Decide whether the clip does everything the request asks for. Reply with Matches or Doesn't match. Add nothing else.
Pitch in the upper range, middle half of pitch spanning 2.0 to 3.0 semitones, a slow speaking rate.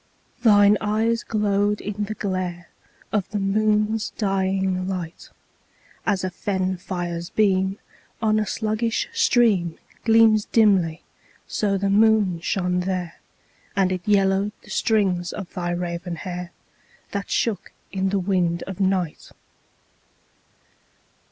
Matches